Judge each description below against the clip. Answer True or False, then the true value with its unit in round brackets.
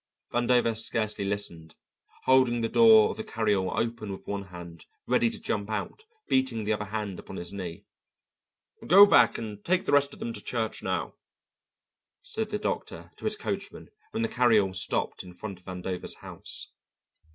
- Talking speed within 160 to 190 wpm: True (180 wpm)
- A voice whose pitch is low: True (110 Hz)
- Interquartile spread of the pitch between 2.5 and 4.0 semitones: False (4.4 semitones)